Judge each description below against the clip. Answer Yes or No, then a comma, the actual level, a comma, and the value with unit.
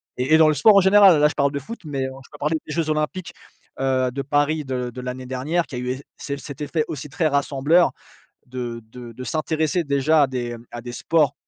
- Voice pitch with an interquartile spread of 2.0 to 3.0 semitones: No, average, 3.4 semitones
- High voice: No, medium, 140 Hz